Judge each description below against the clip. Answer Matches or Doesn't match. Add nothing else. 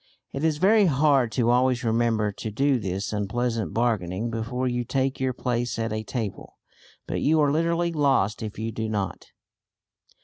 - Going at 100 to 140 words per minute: Doesn't match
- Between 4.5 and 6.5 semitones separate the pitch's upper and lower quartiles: Doesn't match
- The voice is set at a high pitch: Doesn't match